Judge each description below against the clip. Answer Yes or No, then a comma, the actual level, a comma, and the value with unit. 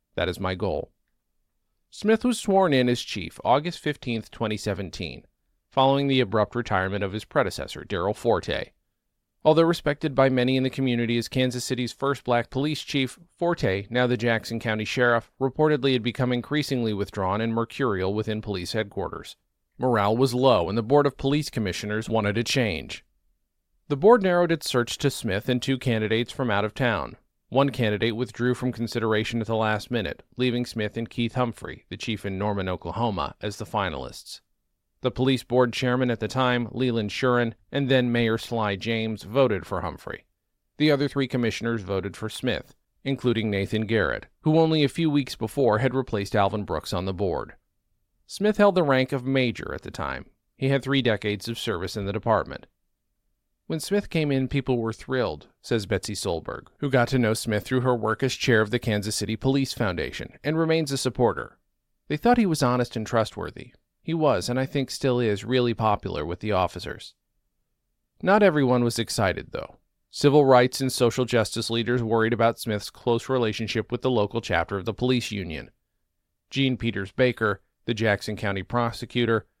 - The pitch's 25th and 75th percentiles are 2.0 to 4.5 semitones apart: Yes, average, 3.5 semitones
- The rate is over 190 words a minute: No, average, 180 wpm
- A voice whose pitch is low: Yes, low, 120 Hz